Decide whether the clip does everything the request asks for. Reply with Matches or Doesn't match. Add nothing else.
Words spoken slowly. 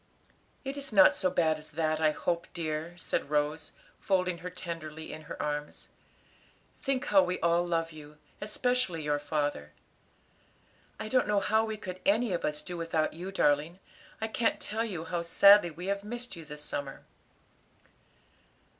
Doesn't match